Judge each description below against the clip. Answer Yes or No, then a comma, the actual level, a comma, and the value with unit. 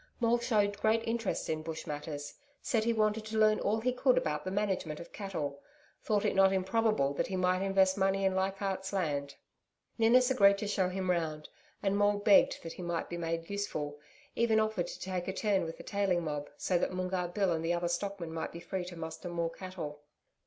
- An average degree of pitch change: Yes, average, 3.6 semitones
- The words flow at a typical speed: No, fast, 210 wpm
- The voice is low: No, high, 190 Hz